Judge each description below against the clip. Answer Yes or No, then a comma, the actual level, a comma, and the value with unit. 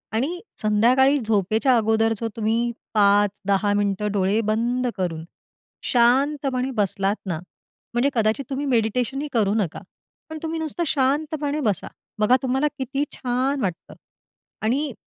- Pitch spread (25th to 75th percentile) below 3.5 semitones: No, average, 4.6 semitones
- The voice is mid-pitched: No, high, 235 Hz